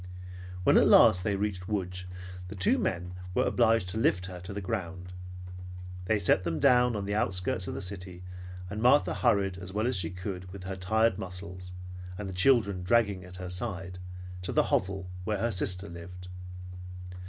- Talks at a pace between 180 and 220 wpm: Yes, average, 185 wpm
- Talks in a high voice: No, very low, 95 Hz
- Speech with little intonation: Yes, narrow, 2.3 semitones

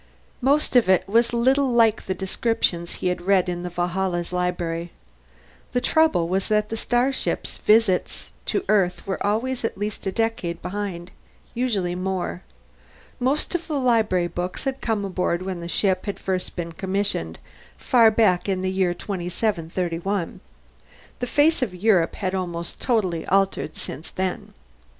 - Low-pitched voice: No, high, 190 Hz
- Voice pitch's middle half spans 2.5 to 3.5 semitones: No, average, 4.2 semitones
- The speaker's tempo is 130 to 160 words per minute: Yes, average, 155 wpm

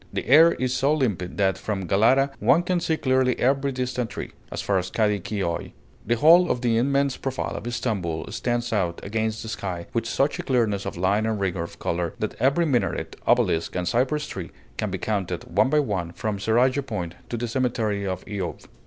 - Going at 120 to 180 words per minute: No, fast, 205 wpm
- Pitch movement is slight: No, average, 5.2 semitones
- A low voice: Yes, low, 110 Hz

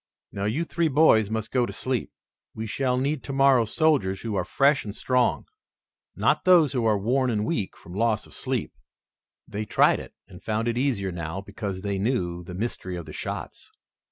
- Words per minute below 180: No, average, 190 wpm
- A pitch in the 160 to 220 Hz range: No, low, 110 Hz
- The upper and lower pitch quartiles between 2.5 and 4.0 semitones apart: No, average, 5.1 semitones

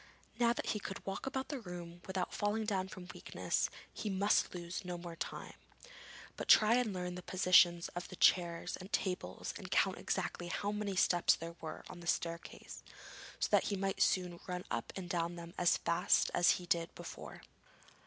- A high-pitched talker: No, medium, 180 Hz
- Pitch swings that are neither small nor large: No, narrow, 2.3 semitones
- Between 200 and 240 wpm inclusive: No, average, 190 wpm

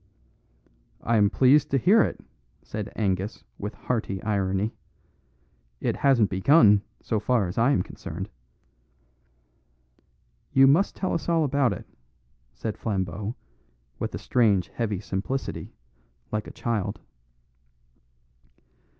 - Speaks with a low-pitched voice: Yes, low, 110 Hz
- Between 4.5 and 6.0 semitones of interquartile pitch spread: Yes, average, 5.2 semitones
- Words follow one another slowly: Yes, slow, 115 wpm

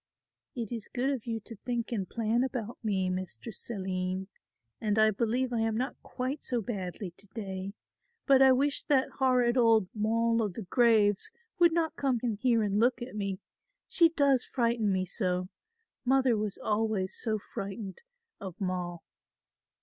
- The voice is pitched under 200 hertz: No, high, 225 Hz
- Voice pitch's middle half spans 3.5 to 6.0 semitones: Yes, average, 4.0 semitones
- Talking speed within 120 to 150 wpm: No, average, 165 wpm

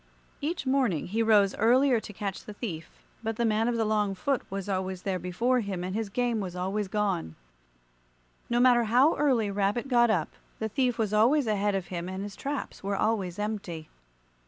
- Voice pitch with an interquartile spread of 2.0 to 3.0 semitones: No, average, 3.7 semitones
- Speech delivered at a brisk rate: No, average, 195 wpm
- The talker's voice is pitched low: No, high, 210 Hz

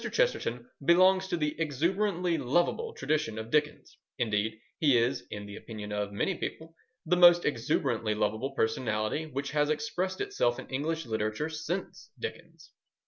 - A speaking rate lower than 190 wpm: Yes, average, 145 wpm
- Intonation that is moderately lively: No, wide, 7.6 semitones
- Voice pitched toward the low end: No, medium, 150 Hz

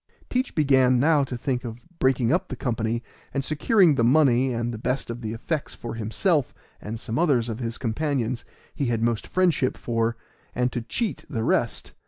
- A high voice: No, low, 125 Hz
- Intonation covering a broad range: No, average, 3.9 semitones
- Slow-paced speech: No, average, 190 wpm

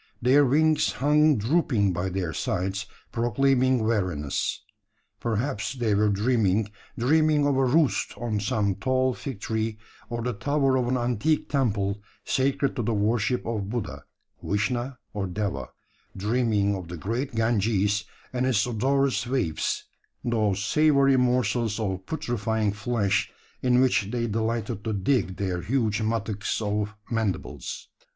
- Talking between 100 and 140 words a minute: Yes, slow, 135 wpm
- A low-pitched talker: Yes, low, 115 Hz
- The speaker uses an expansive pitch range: No, average, 4.0 semitones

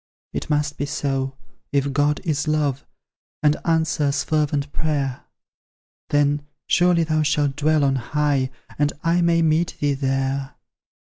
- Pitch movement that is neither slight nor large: No, narrow, 1.9 semitones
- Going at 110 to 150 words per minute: Yes, slow, 135 wpm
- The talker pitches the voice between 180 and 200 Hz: No, medium, 145 Hz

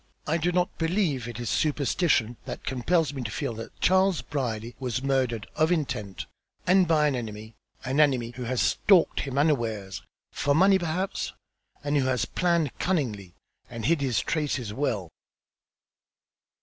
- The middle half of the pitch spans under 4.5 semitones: No, wide, 5.5 semitones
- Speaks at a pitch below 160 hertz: Yes, low, 135 Hz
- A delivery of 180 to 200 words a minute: No, average, 155 wpm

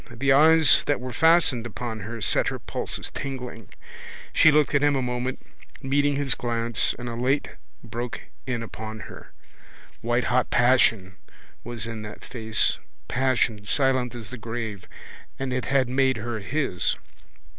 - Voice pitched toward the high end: No, low, 125 Hz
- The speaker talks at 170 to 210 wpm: No, average, 150 wpm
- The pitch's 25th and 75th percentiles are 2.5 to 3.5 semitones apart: Yes, average, 2.8 semitones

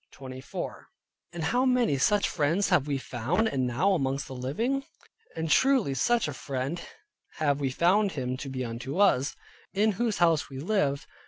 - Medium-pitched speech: Yes, medium, 150 Hz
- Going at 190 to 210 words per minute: No, average, 165 wpm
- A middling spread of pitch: No, wide, 7.2 semitones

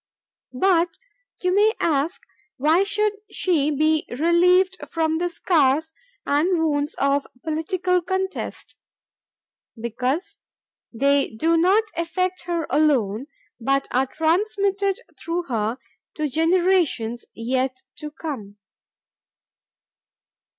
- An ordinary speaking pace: No, slow, 100 wpm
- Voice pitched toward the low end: No, very high, 320 Hz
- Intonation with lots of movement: No, average, 4.7 semitones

